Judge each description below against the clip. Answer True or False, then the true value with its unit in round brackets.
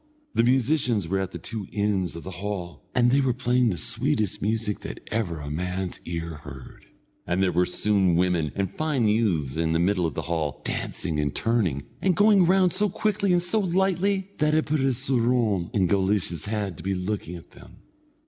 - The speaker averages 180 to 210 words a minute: True (200 wpm)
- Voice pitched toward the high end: False (105 Hz)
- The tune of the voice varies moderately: False (7.0 semitones)